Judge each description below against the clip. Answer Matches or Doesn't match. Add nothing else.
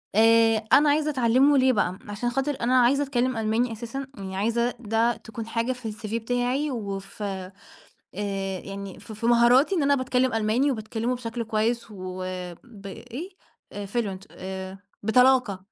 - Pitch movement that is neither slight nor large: Matches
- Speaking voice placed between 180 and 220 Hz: Doesn't match